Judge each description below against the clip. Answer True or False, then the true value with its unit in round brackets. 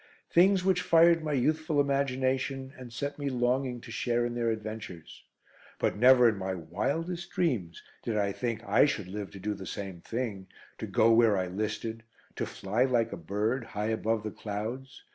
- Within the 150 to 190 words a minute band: True (180 wpm)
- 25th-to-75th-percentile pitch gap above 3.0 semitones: True (4.3 semitones)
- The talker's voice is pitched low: True (120 Hz)